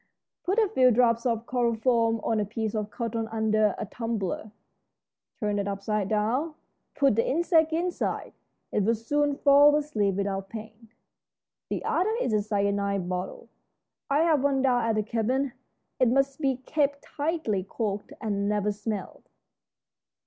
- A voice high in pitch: Yes, high, 230 Hz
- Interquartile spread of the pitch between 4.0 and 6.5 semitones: Yes, average, 4.8 semitones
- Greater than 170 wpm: No, average, 150 wpm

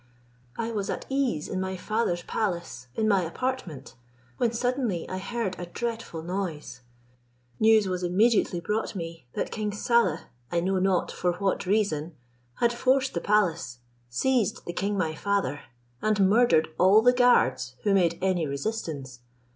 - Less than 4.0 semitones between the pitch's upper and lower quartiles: No, average, 4.6 semitones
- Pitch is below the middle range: No, high, 195 Hz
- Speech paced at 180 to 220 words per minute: No, average, 155 wpm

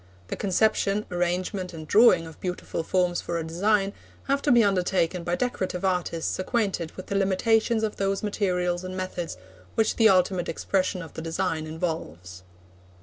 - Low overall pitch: No, medium, 185 Hz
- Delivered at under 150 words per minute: No, average, 160 wpm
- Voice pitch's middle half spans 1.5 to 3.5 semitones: Yes, average, 2.7 semitones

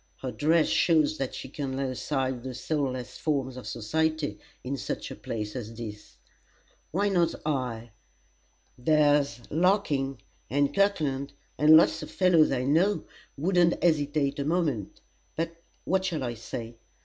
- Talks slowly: No, average, 145 wpm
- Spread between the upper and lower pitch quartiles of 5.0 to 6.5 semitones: No, average, 4.0 semitones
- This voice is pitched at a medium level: Yes, medium, 145 Hz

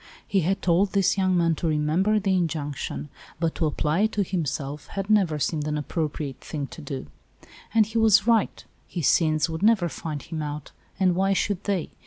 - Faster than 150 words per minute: Yes, average, 200 wpm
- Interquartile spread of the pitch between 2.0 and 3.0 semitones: No, average, 4.3 semitones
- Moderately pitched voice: Yes, medium, 170 Hz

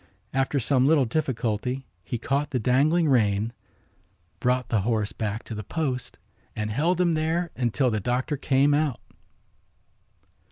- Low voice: Yes, low, 130 Hz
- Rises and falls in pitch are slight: No, average, 4.4 semitones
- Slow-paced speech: No, average, 145 wpm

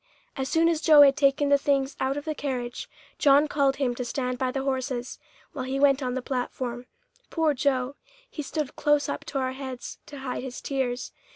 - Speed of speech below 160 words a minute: No, fast, 205 wpm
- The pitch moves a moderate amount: No, narrow, 2.0 semitones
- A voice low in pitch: No, very high, 270 Hz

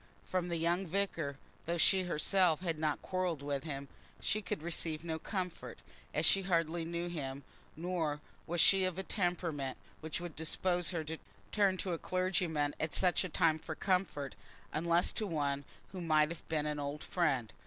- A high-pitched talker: No, medium, 165 Hz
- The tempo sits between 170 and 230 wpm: Yes, average, 180 wpm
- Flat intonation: No, average, 3.0 semitones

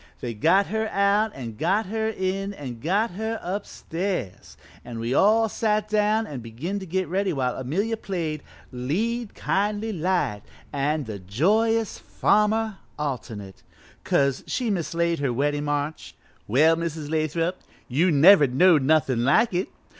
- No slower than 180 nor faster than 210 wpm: No, average, 145 wpm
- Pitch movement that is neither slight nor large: No, wide, 6.8 semitones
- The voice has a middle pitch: Yes, medium, 170 Hz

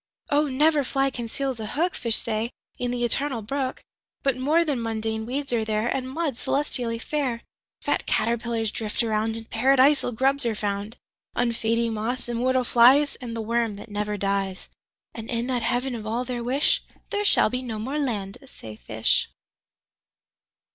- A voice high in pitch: Yes, high, 235 Hz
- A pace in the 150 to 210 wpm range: No, average, 140 wpm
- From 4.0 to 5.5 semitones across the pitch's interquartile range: No, average, 3.2 semitones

